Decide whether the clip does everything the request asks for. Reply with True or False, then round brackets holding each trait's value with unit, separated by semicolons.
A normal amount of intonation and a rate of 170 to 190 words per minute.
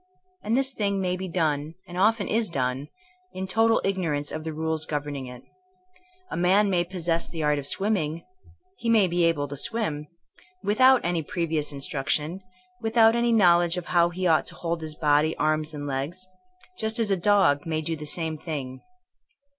True (4.8 semitones; 185 wpm)